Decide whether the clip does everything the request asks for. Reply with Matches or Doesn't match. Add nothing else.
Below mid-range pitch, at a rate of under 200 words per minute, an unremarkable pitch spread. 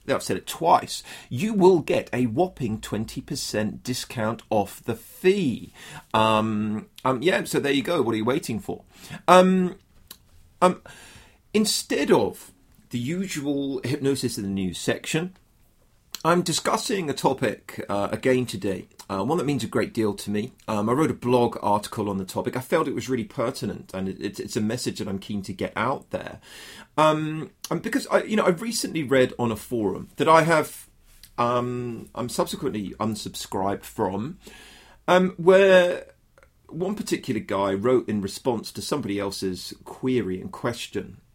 Doesn't match